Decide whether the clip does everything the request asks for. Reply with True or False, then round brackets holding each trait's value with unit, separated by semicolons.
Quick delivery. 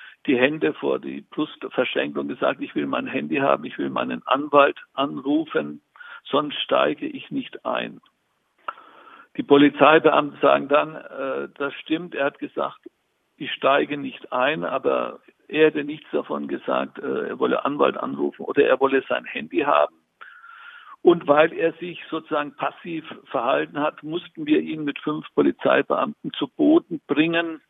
False (155 wpm)